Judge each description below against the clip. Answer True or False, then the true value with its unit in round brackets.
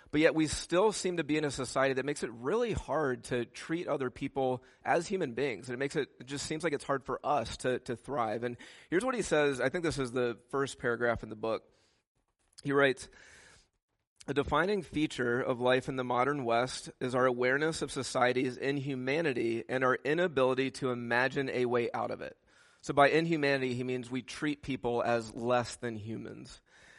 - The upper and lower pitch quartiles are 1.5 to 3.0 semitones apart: True (2.7 semitones)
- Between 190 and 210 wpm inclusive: True (200 wpm)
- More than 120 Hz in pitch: True (130 Hz)